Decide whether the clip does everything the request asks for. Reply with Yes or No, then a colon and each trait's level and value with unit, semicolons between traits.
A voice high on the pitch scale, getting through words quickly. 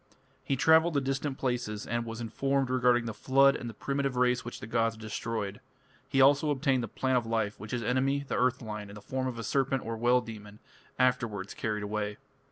No: low, 125 Hz; fast, 210 wpm